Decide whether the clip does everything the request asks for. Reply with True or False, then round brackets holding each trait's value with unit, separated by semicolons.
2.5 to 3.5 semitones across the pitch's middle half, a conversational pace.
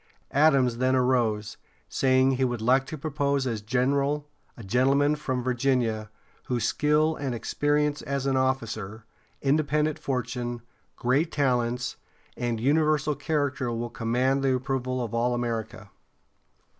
False (2.8 semitones; 130 wpm)